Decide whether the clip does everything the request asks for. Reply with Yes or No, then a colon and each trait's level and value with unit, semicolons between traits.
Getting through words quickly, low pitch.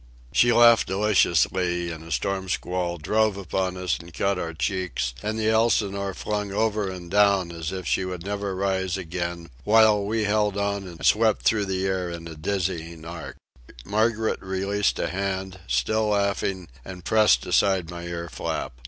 No: average, 170 wpm; very low, 95 Hz